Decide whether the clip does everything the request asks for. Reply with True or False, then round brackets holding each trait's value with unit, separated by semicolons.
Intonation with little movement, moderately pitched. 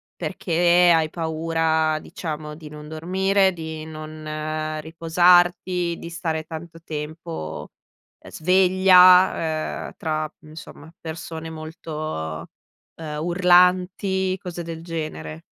True (2.1 semitones; 160 Hz)